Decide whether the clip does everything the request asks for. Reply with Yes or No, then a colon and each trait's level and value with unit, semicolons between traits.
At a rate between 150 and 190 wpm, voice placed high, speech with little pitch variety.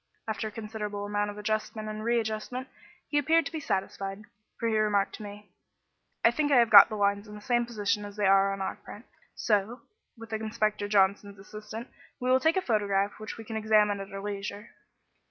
No: fast, 205 wpm; high, 210 Hz; narrow, 1.9 semitones